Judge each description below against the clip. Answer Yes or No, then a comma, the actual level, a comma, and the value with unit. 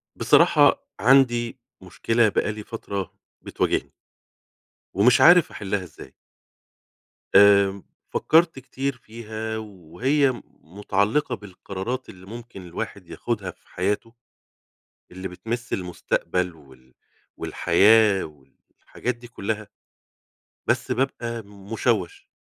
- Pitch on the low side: Yes, low, 105 Hz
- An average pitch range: Yes, average, 4.0 semitones